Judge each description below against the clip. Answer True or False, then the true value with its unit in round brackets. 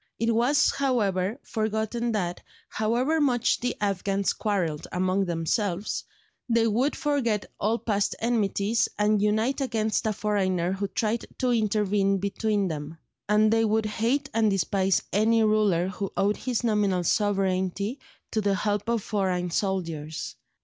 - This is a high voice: True (210 Hz)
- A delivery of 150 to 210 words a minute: False (140 wpm)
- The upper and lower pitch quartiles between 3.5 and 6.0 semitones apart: False (2.8 semitones)